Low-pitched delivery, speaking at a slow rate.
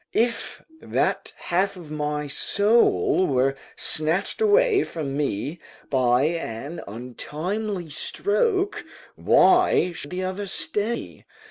No: medium, 170 Hz; slow, 105 wpm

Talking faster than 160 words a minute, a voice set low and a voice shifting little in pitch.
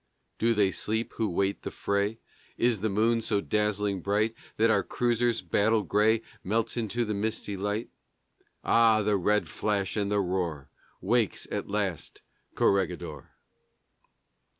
No: average, 140 wpm; low, 105 Hz; narrow, 2.1 semitones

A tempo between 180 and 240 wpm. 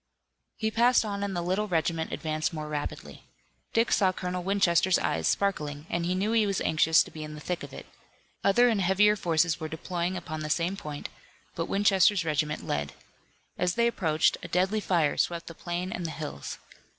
Yes: average, 195 wpm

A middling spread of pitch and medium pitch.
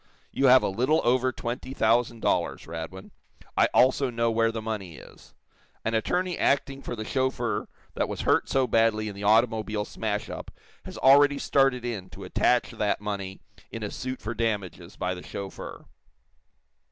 No: average, 3.7 semitones; low, 115 Hz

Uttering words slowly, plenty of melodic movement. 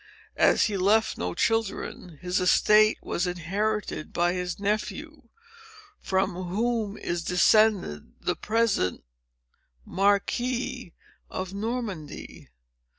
No: slow, 95 wpm; average, 3.8 semitones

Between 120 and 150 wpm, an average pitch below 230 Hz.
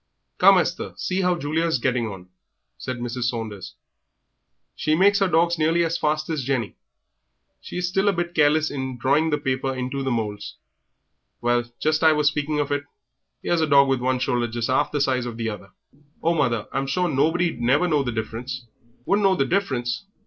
No: average, 200 wpm; medium, 140 Hz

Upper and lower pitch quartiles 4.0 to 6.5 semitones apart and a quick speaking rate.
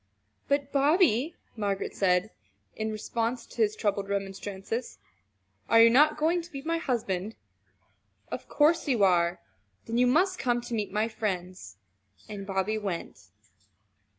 No: wide, 5.6 semitones; average, 145 wpm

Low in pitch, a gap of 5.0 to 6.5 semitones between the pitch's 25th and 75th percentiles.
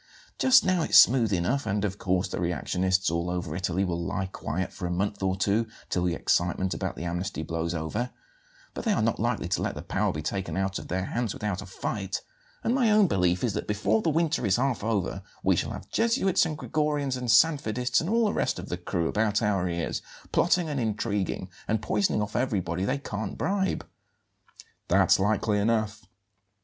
Yes: low, 100 Hz; average, 5.3 semitones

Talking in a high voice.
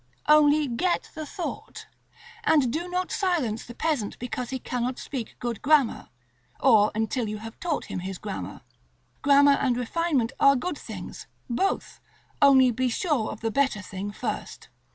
Yes: very high, 260 Hz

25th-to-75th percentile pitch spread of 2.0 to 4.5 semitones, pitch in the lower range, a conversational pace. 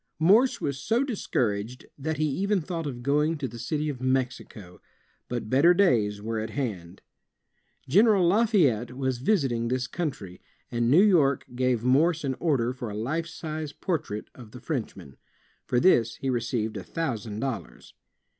No: wide, 5.6 semitones; low, 130 Hz; average, 160 wpm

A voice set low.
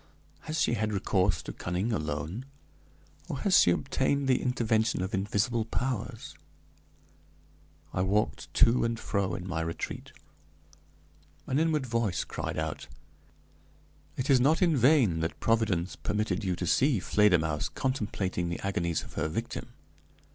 Yes: low, 105 Hz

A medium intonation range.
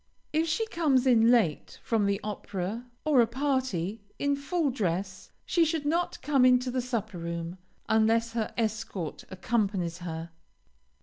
No: wide, 6.0 semitones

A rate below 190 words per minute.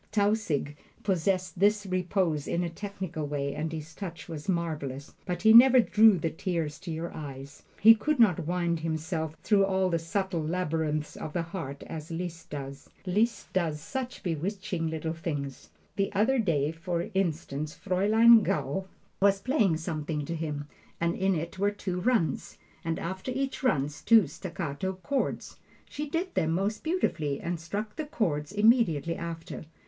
Yes: average, 160 wpm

